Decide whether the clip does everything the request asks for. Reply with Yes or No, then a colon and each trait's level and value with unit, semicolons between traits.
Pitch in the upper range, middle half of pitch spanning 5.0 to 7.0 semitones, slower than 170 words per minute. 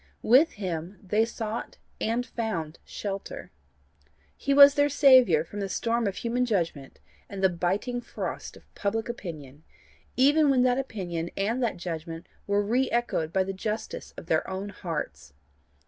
Yes: high, 205 Hz; wide, 5.6 semitones; average, 155 wpm